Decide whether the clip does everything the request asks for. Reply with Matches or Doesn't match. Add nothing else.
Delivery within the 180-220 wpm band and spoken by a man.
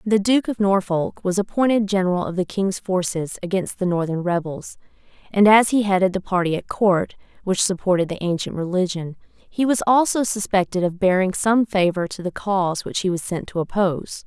Doesn't match